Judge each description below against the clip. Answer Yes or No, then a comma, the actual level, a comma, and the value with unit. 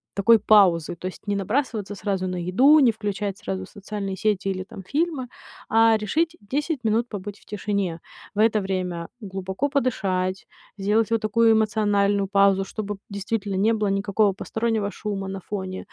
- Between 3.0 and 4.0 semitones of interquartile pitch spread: No, narrow, 2.5 semitones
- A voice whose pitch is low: No, high, 205 Hz